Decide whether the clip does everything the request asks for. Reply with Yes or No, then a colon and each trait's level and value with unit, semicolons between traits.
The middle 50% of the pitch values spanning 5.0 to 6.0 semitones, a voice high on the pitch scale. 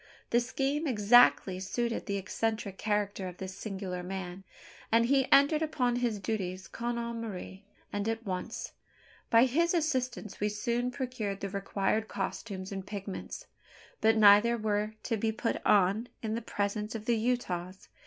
No: average, 3.3 semitones; high, 215 Hz